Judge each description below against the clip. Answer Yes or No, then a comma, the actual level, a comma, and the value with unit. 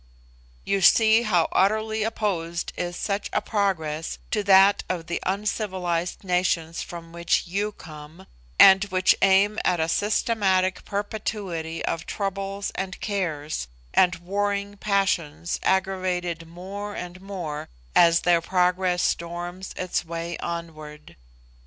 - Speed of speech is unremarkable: No, slow, 120 wpm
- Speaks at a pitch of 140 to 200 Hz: Yes, medium, 185 Hz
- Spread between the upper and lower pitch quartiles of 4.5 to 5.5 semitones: No, average, 2.9 semitones